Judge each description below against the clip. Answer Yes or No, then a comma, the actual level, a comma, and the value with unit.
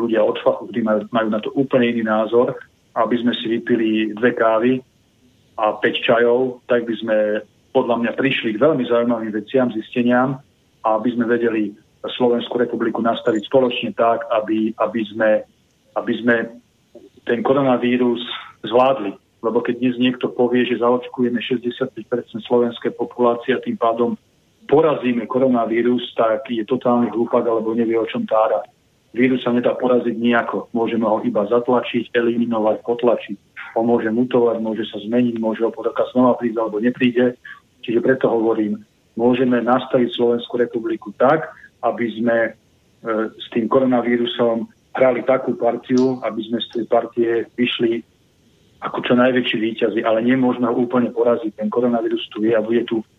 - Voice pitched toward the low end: Yes, low, 120 Hz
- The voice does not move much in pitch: Yes, narrow, 1.5 semitones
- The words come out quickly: No, average, 150 wpm